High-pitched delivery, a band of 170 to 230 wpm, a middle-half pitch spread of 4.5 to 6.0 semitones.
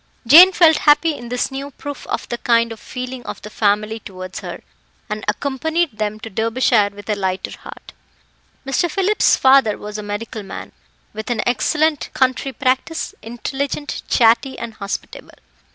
No: high, 240 Hz; average, 155 wpm; average, 4.8 semitones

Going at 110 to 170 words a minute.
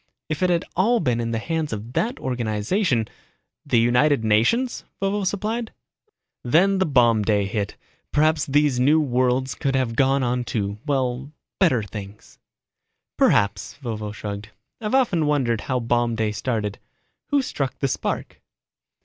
Yes: average, 155 wpm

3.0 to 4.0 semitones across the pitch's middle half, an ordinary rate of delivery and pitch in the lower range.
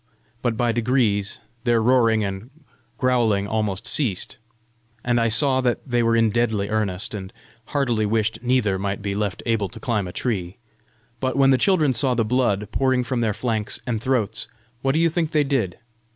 Yes: average, 3.5 semitones; average, 180 wpm; low, 115 Hz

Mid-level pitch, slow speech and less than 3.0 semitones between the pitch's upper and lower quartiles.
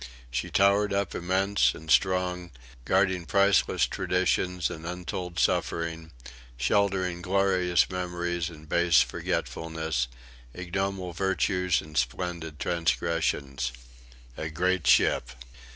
No: very low, 90 Hz; slow, 100 wpm; narrow, 2.5 semitones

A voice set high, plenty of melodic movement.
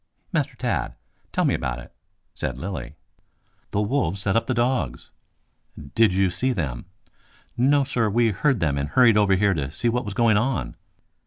No: low, 105 Hz; wide, 7.1 semitones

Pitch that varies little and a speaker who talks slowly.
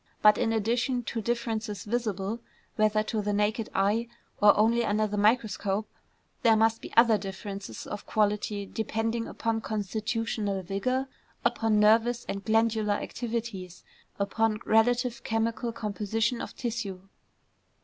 Yes: narrow, 1.9 semitones; slow, 130 wpm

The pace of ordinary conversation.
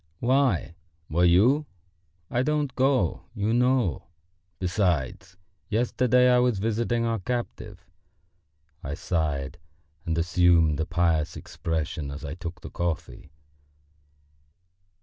No: slow, 110 wpm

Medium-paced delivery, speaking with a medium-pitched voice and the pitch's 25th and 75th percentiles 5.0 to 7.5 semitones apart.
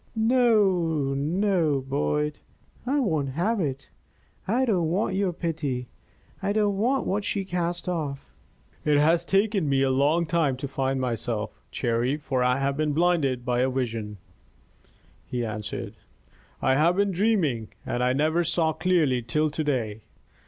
Yes: average, 150 wpm; medium, 150 Hz; wide, 5.5 semitones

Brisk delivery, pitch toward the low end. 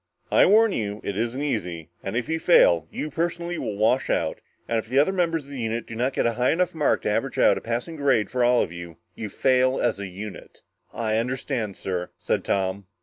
Yes: fast, 230 wpm; low, 120 Hz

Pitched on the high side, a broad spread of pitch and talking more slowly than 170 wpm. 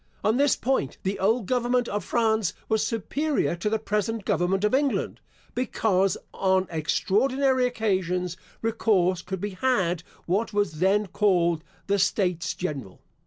No: high, 205 Hz; average, 3.9 semitones; average, 140 wpm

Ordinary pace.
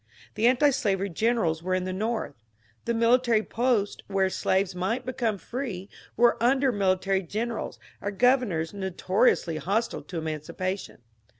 No: slow, 130 wpm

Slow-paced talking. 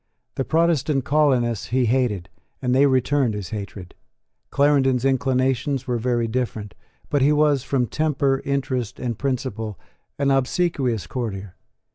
Yes: slow, 130 wpm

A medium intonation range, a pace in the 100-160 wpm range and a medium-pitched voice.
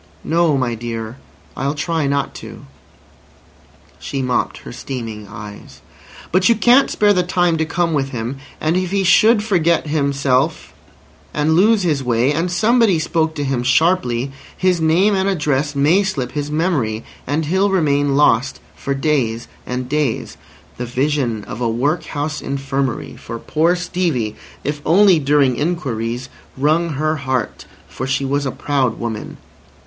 Yes: average, 4.9 semitones; average, 150 wpm; medium, 145 Hz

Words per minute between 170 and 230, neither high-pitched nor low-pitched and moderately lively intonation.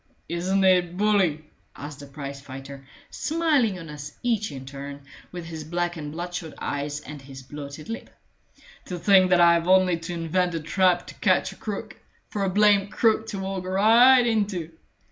Yes: average, 175 wpm; medium, 175 Hz; average, 4.8 semitones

